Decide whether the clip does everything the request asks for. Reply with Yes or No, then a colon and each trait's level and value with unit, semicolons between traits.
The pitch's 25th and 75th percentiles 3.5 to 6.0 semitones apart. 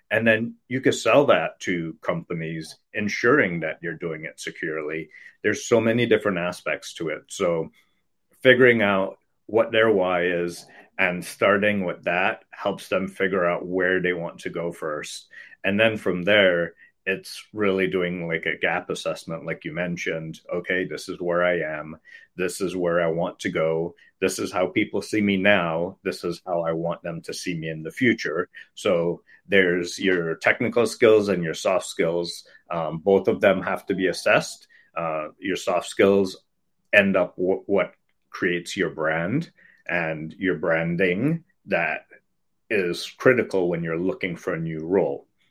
No: average, 3.0 semitones